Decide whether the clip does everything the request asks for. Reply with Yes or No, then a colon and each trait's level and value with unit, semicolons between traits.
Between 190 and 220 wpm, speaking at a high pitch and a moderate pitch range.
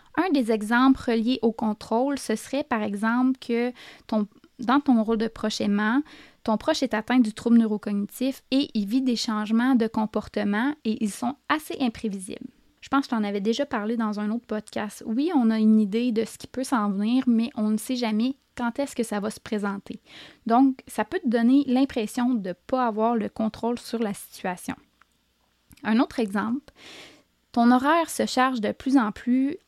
Yes: average, 200 wpm; high, 235 Hz; average, 3.1 semitones